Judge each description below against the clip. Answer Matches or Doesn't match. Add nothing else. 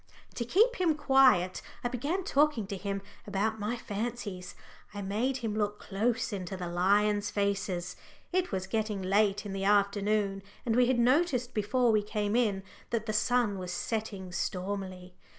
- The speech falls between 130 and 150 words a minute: Doesn't match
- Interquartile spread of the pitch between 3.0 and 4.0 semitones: Matches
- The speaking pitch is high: Matches